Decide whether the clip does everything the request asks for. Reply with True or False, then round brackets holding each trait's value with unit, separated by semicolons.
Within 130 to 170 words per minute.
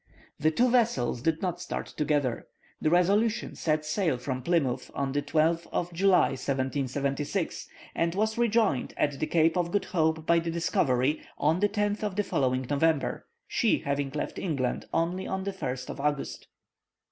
True (160 wpm)